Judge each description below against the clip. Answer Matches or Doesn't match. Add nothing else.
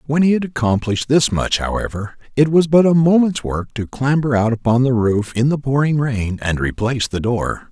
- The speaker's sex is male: Matches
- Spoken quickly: Matches